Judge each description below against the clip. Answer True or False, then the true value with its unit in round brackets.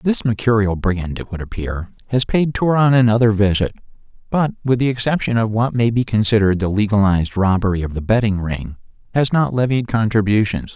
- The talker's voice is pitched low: True (110 Hz)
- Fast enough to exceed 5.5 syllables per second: True (5.8 syllables/s)